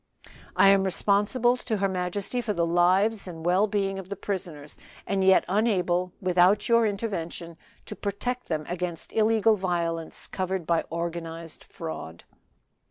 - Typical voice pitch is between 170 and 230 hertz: Yes, high, 190 Hz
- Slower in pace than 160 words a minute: Yes, average, 145 wpm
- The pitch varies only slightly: No, average, 3.2 semitones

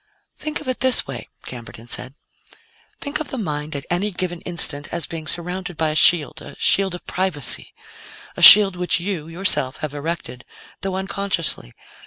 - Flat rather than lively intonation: No, average, 4.2 semitones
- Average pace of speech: Yes, average, 170 wpm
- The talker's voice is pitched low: No, medium, 175 Hz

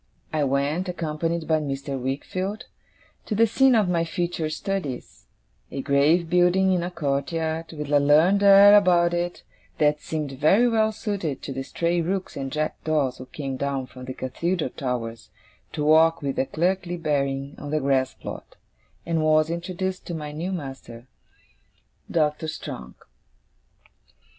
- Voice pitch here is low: No, medium, 155 Hz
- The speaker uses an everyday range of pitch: Yes, average, 4.1 semitones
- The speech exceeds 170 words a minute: No, average, 155 wpm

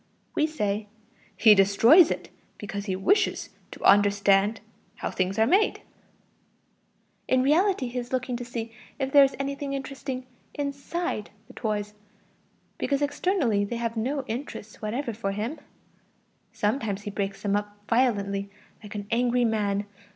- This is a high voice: Yes, high, 230 Hz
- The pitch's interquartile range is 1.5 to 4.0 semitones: No, average, 5.0 semitones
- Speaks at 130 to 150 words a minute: Yes, average, 145 wpm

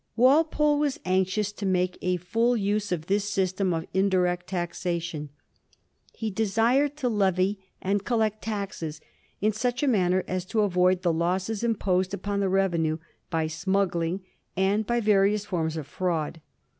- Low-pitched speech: No, high, 190 Hz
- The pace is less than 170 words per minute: Yes, average, 150 wpm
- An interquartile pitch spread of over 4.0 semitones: No, average, 3.2 semitones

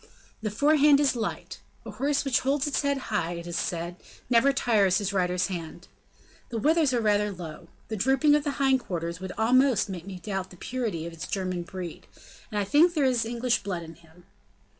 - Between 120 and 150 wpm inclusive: No, fast, 205 wpm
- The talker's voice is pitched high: Yes, high, 210 Hz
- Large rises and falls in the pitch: Yes, wide, 7.0 semitones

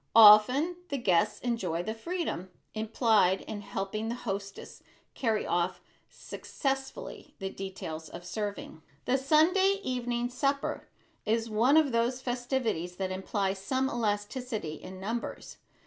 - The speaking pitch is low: No, high, 225 Hz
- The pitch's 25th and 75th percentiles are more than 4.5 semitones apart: Yes, average, 4.9 semitones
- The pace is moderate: No, slow, 125 wpm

